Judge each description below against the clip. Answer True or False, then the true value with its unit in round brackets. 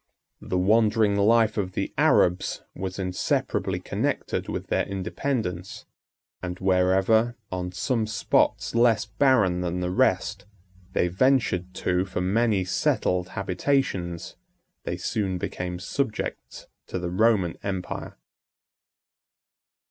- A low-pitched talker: True (95 Hz)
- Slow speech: True (110 wpm)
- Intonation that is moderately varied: True (3.5 semitones)